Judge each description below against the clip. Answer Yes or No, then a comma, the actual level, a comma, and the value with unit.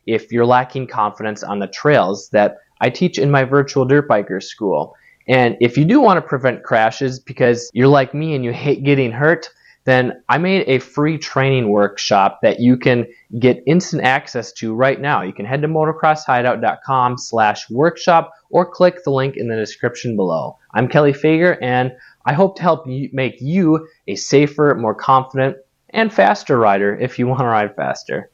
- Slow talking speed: No, average, 180 wpm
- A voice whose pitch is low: Yes, low, 130 Hz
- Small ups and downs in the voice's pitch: No, average, 3.7 semitones